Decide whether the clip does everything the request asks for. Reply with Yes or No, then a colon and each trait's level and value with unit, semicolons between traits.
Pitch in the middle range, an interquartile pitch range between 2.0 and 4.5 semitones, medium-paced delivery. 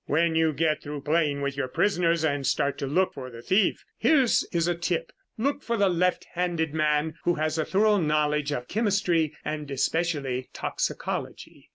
Yes: medium, 160 Hz; average, 3.3 semitones; average, 180 wpm